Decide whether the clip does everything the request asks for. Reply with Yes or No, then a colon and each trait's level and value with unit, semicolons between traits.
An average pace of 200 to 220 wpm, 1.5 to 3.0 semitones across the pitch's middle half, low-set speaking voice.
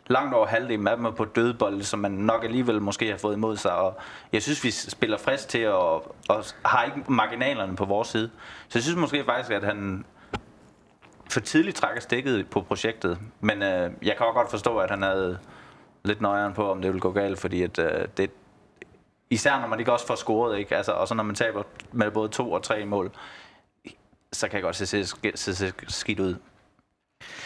Yes: average, 210 wpm; narrow, 2.5 semitones; low, 105 Hz